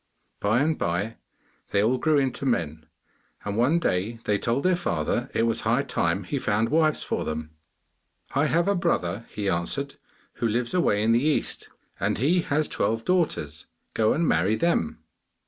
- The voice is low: Yes, low, 115 Hz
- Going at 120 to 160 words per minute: No, average, 175 wpm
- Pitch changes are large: Yes, wide, 7.2 semitones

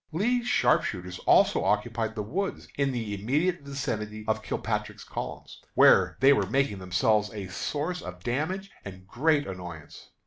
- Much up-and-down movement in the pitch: Yes, wide, 6.4 semitones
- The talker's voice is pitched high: No, low, 115 Hz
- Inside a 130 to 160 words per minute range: Yes, average, 145 wpm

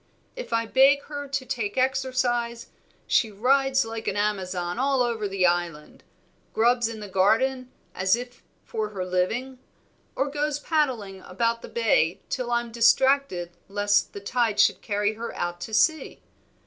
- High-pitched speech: Yes, high, 230 Hz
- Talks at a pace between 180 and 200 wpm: No, average, 155 wpm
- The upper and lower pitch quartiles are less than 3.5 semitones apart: No, average, 4.6 semitones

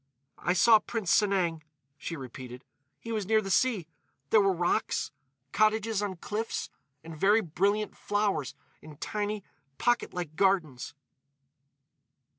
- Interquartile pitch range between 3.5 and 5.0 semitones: No, wide, 5.4 semitones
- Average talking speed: No, slow, 115 wpm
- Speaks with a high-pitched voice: Yes, high, 195 Hz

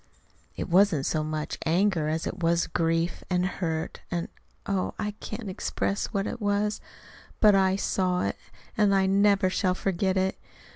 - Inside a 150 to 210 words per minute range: Yes, average, 160 wpm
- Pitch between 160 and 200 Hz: Yes, high, 190 Hz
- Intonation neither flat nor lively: Yes, average, 3.0 semitones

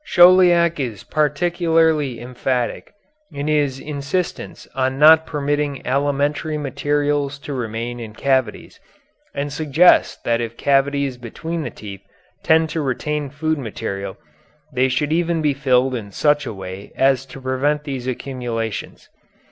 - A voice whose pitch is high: No, medium, 140 Hz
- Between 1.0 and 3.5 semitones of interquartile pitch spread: Yes, average, 3.1 semitones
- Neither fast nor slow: No, slow, 130 wpm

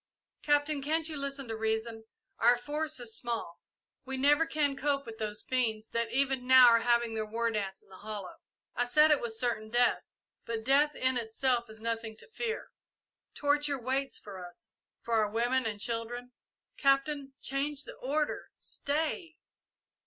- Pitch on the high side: Yes, high, 245 Hz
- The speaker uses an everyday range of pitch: Yes, average, 4.0 semitones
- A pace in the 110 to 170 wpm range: Yes, average, 165 wpm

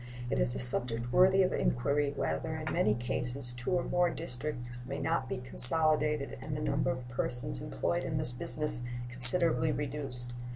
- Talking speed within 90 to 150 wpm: No, average, 170 wpm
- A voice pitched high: No, low, 130 Hz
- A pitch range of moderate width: Yes, average, 3.8 semitones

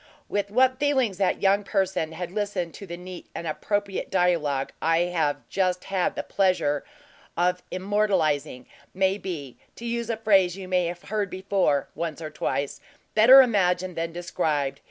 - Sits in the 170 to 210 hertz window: Yes, medium, 185 Hz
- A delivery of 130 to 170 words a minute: Yes, average, 160 wpm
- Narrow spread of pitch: No, average, 3.3 semitones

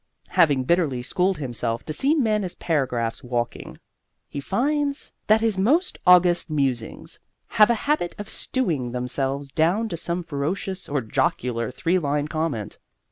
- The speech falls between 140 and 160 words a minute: Yes, average, 145 wpm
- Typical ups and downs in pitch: No, wide, 7.0 semitones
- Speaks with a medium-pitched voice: Yes, medium, 160 Hz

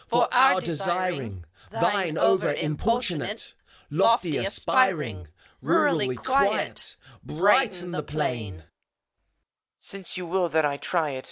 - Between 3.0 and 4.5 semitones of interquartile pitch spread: No, average, 4.9 semitones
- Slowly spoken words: Yes, slow, 110 wpm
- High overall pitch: No, medium, 175 Hz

